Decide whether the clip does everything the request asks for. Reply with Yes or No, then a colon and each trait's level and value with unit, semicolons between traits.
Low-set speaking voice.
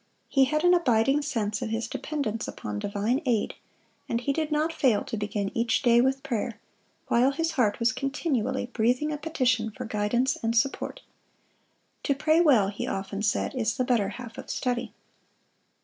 No: high, 245 Hz